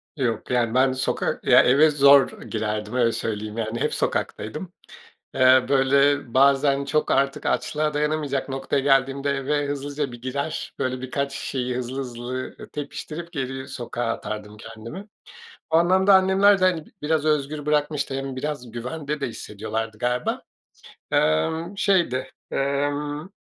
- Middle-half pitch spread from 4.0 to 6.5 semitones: No, average, 3.3 semitones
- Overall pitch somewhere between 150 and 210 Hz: No, low, 135 Hz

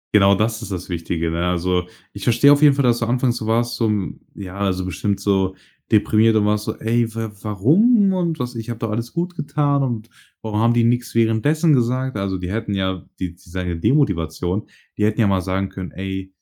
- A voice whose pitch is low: Yes, low, 110 Hz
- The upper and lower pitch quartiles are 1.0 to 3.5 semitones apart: No, average, 4.3 semitones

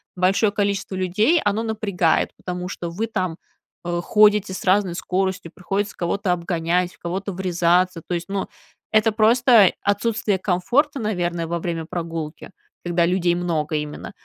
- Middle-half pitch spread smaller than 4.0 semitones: Yes, average, 3.0 semitones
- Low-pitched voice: No, medium, 185 Hz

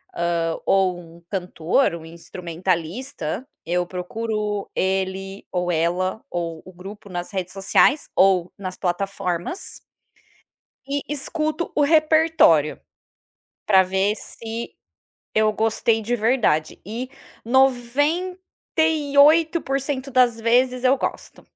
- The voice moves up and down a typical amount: No, wide, 6.8 semitones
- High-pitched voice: Yes, high, 210 Hz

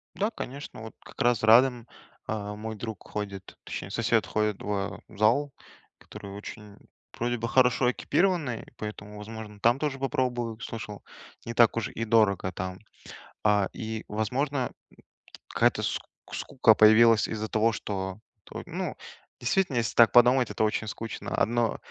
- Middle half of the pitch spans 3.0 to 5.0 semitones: No, narrow, 2.5 semitones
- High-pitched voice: No, low, 110 Hz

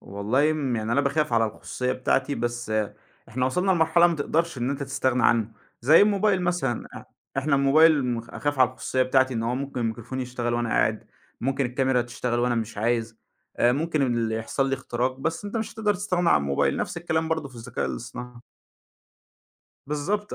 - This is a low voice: Yes, low, 130 Hz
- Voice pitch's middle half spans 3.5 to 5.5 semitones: Yes, average, 4.7 semitones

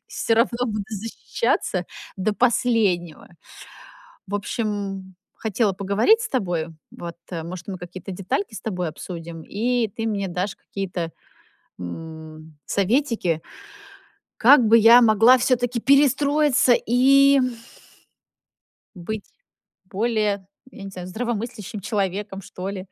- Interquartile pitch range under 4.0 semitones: No, average, 4.5 semitones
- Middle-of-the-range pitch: No, high, 205 Hz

